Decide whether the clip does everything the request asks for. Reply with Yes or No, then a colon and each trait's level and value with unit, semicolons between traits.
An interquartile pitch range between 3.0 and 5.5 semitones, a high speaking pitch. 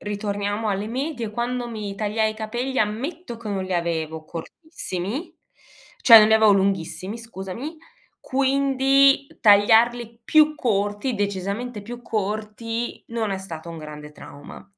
Yes: average, 3.5 semitones; high, 215 Hz